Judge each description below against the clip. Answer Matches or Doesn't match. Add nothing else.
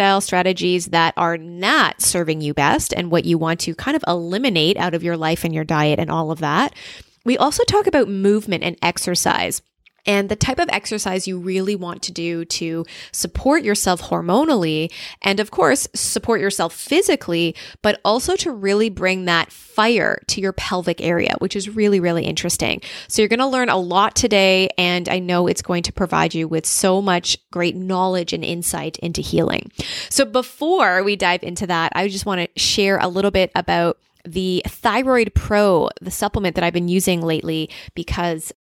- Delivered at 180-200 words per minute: Matches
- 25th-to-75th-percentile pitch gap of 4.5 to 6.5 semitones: Doesn't match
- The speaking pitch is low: Doesn't match